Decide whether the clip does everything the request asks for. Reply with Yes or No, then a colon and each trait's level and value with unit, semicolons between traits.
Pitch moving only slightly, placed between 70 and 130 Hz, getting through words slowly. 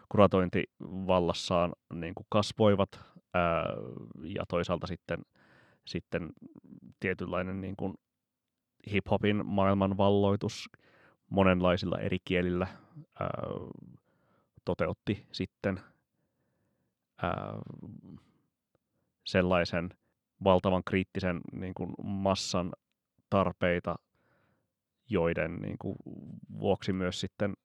Yes: narrow, 1.8 semitones; very low, 95 Hz; slow, 75 wpm